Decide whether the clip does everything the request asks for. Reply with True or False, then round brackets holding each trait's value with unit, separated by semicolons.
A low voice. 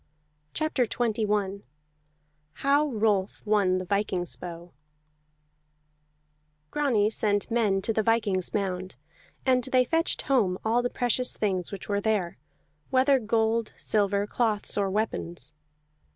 False (210 Hz)